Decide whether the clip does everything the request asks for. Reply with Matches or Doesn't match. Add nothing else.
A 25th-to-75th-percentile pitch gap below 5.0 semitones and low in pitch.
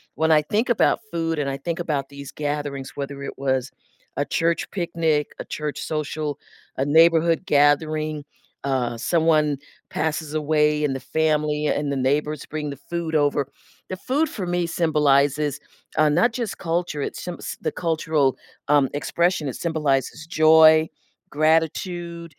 Doesn't match